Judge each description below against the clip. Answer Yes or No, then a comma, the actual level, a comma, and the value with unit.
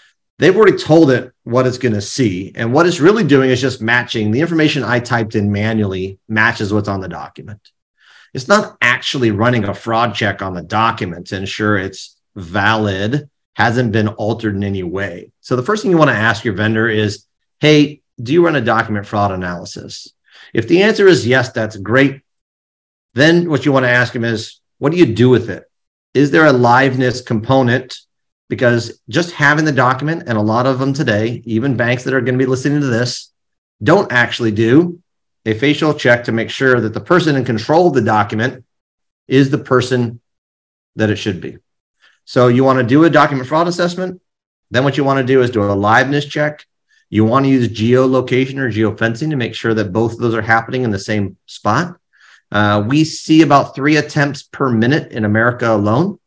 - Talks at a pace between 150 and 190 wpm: No, average, 200 wpm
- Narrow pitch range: No, average, 4.4 semitones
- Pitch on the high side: No, low, 120 Hz